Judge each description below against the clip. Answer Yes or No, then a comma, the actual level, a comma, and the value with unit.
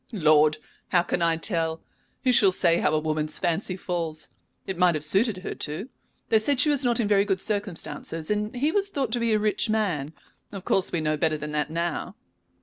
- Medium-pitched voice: Yes, medium, 180 Hz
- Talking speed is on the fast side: Yes, fast, 215 wpm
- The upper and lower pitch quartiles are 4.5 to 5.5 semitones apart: Yes, average, 5.1 semitones